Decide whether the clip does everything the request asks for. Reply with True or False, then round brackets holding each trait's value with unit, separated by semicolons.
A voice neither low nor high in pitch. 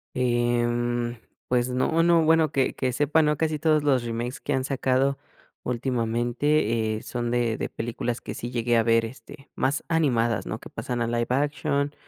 False (125 Hz)